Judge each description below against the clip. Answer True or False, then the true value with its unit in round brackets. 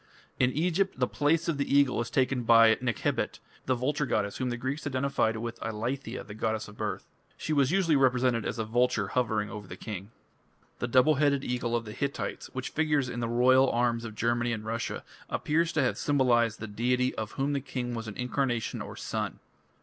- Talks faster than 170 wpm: True (205 wpm)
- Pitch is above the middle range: False (125 Hz)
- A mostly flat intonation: False (3.3 semitones)